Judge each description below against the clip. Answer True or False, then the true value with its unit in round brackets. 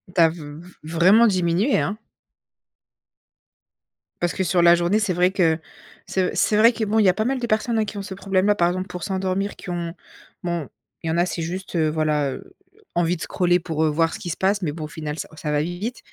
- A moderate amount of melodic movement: True (3.3 semitones)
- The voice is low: False (180 Hz)